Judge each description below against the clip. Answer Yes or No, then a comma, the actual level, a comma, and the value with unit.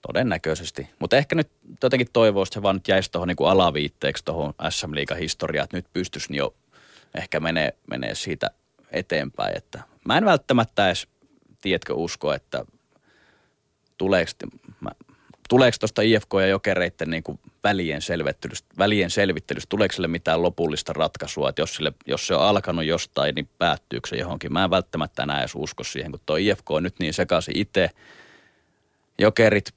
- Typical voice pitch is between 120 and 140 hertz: No, very low, 90 Hz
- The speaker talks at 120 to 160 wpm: Yes, average, 150 wpm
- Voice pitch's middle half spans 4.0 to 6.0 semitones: Yes, average, 4.5 semitones